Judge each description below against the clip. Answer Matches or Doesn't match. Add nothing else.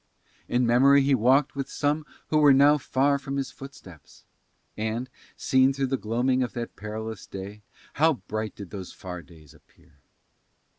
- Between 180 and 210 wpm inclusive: Doesn't match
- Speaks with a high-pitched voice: Doesn't match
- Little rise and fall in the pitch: Doesn't match